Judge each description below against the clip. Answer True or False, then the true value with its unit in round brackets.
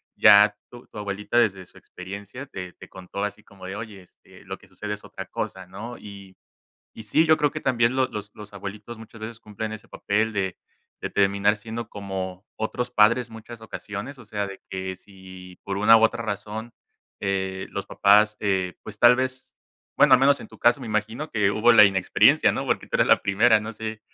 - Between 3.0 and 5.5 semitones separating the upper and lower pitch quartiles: False (2.4 semitones)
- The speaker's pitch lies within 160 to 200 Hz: False (105 Hz)